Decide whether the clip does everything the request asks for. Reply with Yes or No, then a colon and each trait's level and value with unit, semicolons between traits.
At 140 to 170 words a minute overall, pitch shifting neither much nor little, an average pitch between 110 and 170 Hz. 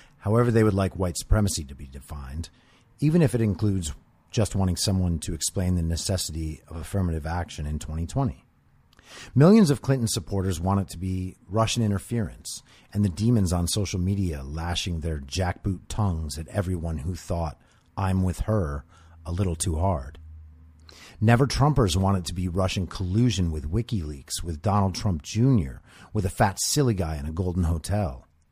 No: average, 165 wpm; average, 4.5 semitones; very low, 95 Hz